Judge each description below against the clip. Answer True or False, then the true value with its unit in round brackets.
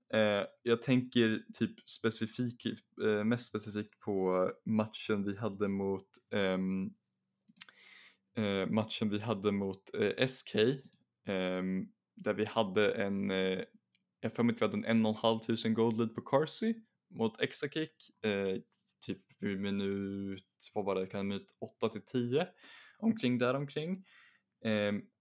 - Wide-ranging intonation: False (3.0 semitones)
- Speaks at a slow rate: True (105 wpm)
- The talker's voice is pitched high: False (110 Hz)